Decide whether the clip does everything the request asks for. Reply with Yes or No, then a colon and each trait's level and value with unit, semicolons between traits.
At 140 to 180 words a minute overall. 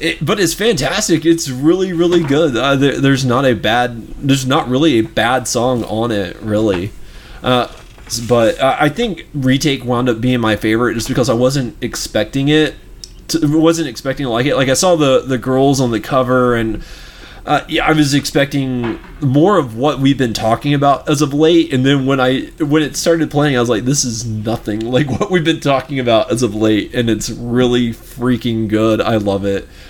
No: fast, 205 wpm